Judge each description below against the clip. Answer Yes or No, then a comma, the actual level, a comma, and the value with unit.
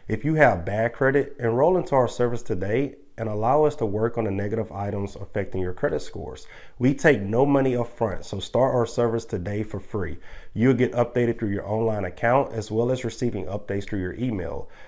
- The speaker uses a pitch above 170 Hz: No, low, 115 Hz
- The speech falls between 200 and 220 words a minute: Yes, fast, 205 wpm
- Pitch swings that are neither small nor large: Yes, average, 3.6 semitones